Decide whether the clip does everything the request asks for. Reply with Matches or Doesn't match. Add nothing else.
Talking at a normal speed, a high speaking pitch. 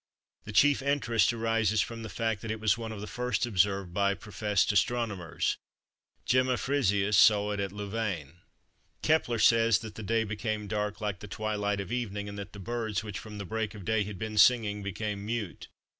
Doesn't match